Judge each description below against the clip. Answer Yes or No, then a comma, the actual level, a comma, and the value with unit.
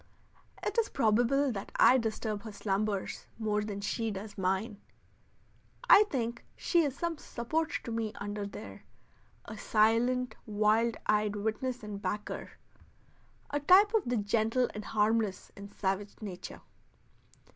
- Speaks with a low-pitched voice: No, high, 220 Hz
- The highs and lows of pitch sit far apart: No, average, 3.2 semitones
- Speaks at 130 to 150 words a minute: Yes, slow, 135 wpm